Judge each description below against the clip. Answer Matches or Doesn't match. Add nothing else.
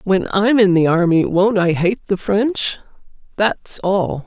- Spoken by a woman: Matches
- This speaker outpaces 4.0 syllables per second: Doesn't match